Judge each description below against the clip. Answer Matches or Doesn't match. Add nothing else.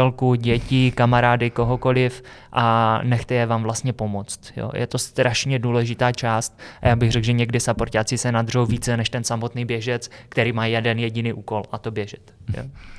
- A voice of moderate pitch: Doesn't match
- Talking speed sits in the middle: Doesn't match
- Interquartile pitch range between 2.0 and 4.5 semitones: Doesn't match